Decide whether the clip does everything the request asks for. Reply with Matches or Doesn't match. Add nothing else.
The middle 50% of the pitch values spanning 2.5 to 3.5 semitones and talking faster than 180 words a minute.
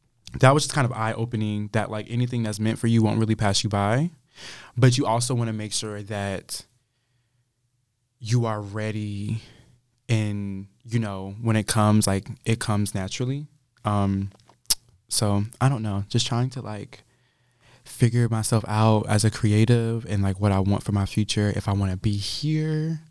Doesn't match